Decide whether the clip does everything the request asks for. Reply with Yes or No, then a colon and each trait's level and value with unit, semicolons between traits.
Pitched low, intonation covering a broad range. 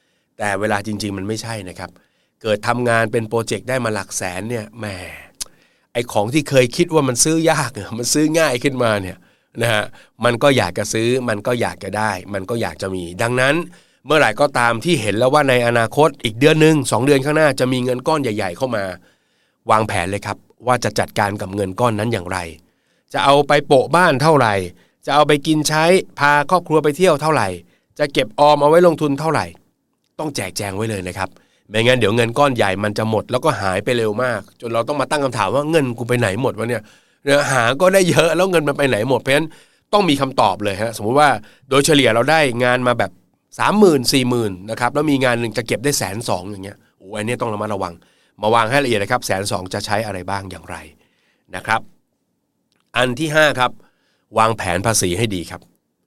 Yes: low, 120 Hz; wide, 5.8 semitones